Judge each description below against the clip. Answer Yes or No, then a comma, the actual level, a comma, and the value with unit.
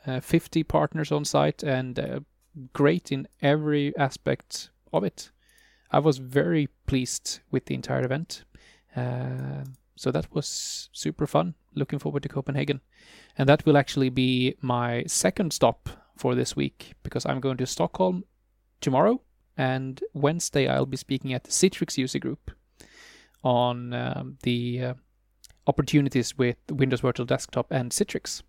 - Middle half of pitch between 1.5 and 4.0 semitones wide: Yes, average, 3.4 semitones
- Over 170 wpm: No, average, 145 wpm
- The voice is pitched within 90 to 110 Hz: No, low, 135 Hz